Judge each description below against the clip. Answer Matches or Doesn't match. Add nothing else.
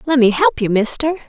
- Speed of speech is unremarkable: Matches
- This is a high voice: Matches